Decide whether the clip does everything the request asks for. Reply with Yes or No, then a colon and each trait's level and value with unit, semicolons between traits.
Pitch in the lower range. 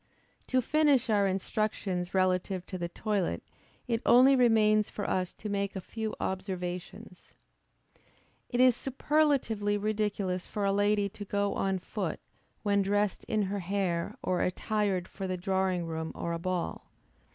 No: high, 200 Hz